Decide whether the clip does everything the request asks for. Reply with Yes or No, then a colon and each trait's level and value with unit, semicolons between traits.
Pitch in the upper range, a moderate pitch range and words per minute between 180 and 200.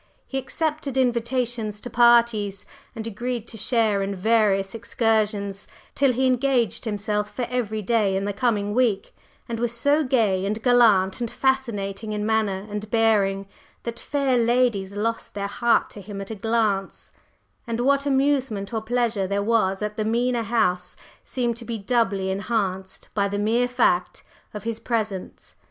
No: high, 225 Hz; average, 3.1 semitones; average, 160 wpm